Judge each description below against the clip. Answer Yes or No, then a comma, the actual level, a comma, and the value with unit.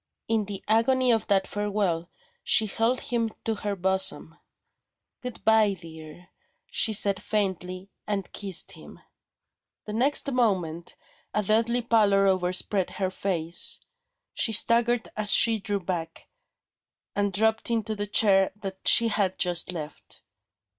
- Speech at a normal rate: No, slow, 130 wpm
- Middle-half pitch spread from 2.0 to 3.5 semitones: Yes, average, 2.9 semitones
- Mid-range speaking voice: No, high, 205 Hz